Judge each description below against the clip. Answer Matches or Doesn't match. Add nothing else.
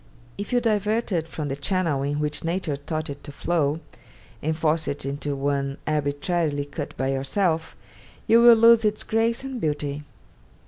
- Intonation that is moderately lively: Doesn't match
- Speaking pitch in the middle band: Matches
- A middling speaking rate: Matches